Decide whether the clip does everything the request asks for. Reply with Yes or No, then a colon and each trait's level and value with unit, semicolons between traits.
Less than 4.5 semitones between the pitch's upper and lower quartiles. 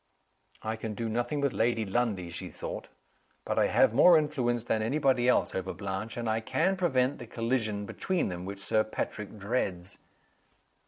Yes: average, 3.8 semitones